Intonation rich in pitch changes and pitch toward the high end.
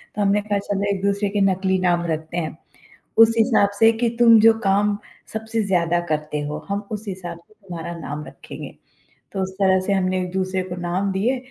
No: average, 3.0 semitones; high, 195 Hz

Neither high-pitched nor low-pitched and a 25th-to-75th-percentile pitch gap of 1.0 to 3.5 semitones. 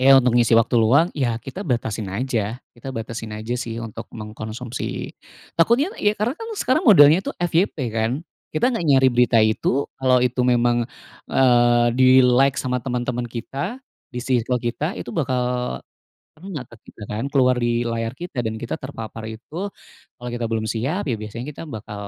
No: low, 125 Hz; average, 3.1 semitones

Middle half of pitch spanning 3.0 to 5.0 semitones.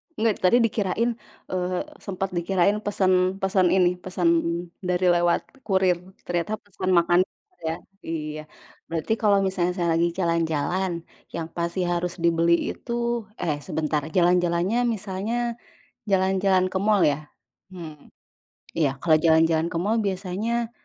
No: narrow, 2.5 semitones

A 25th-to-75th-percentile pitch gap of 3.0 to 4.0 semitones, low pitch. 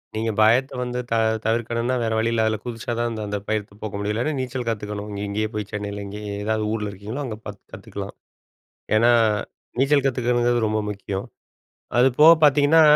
No: narrow, 2.6 semitones; low, 110 Hz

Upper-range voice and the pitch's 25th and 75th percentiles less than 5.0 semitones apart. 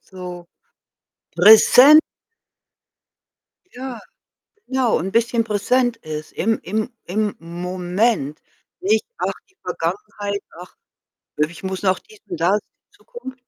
No: high, 210 Hz; average, 5.3 semitones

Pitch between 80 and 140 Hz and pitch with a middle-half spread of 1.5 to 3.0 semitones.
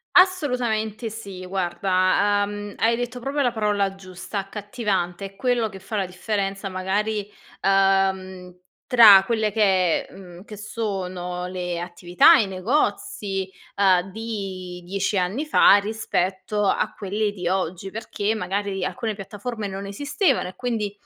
No: high, 200 Hz; average, 2.7 semitones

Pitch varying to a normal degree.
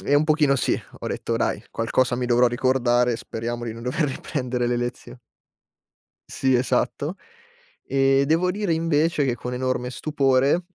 Yes: average, 3.2 semitones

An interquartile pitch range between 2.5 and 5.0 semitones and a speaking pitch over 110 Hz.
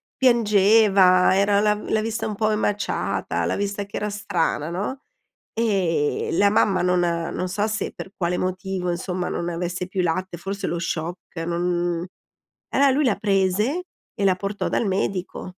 Yes: average, 2.8 semitones; high, 190 Hz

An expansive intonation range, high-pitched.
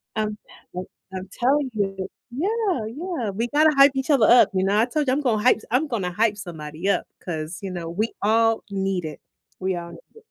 Yes: wide, 5.9 semitones; high, 215 Hz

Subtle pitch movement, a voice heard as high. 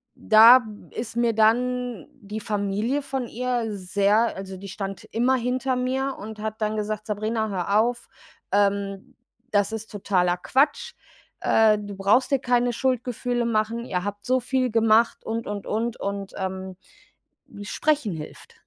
No: average, 3.4 semitones; high, 220 Hz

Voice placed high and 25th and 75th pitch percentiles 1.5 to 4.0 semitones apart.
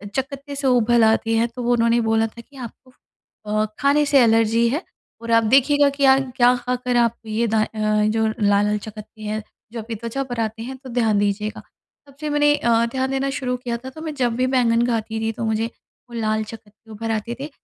Yes: high, 235 Hz; average, 2.8 semitones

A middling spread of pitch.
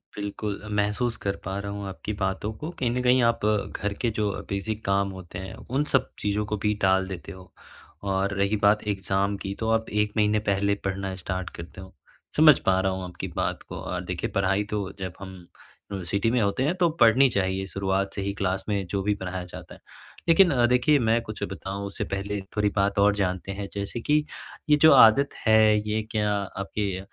No: narrow, 2.1 semitones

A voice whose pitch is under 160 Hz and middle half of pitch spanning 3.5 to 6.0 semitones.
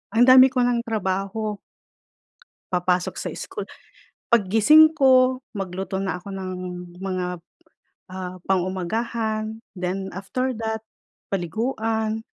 No: high, 215 Hz; average, 3.9 semitones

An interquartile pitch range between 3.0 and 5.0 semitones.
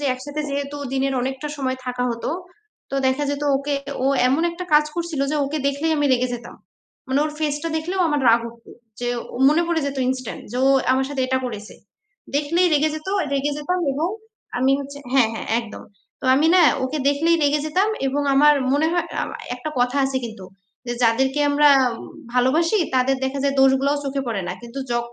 No: narrow, 2.5 semitones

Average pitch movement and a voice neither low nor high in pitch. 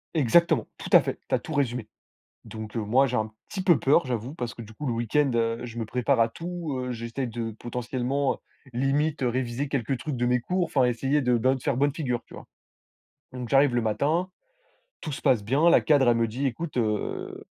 No: average, 3.4 semitones; low, 125 Hz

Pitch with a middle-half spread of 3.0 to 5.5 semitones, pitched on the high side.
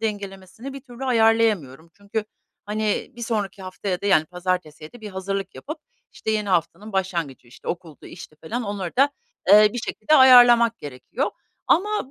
Yes: average, 4.3 semitones; high, 205 Hz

